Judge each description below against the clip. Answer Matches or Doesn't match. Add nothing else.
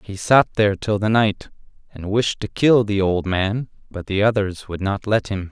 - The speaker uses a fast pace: Matches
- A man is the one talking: Matches